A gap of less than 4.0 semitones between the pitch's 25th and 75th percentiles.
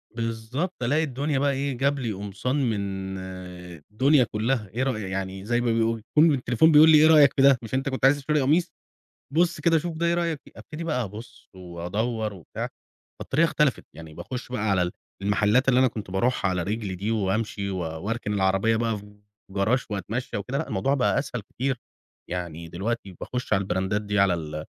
No: wide, 5.6 semitones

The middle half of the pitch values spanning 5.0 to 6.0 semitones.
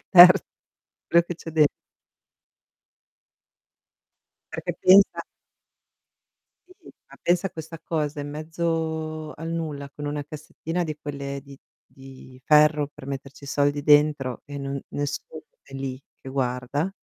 No: narrow, 2.5 semitones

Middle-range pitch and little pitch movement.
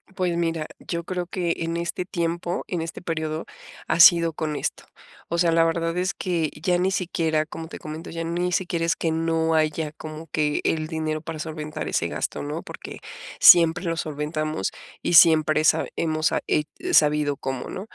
Yes: medium, 165 Hz; narrow, 1.6 semitones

